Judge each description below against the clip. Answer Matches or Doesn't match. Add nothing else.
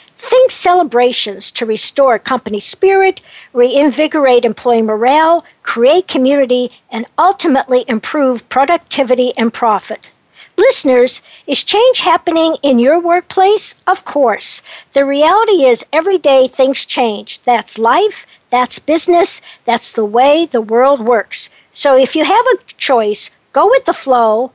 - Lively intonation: Matches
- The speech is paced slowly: Matches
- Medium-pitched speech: Doesn't match